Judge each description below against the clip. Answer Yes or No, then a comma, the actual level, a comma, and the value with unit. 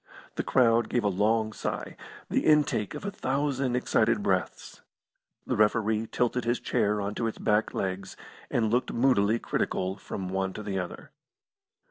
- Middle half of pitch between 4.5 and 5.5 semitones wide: No, average, 3.4 semitones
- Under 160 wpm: No, average, 165 wpm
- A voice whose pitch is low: Yes, low, 110 Hz